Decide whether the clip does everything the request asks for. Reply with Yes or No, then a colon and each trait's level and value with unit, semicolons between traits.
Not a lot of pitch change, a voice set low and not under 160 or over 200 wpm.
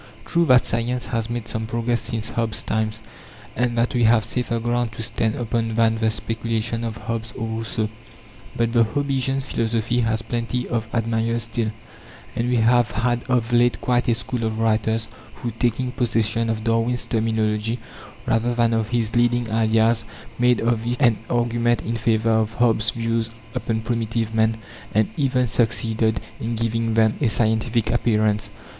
Yes: narrow, 1.2 semitones; low, 115 Hz; average, 165 wpm